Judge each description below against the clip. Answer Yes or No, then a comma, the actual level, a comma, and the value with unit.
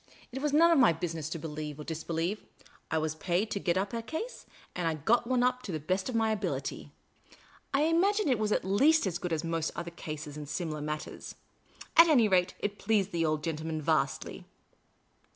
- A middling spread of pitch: No, wide, 6.9 semitones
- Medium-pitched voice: Yes, medium, 180 Hz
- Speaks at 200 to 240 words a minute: Yes, fast, 205 wpm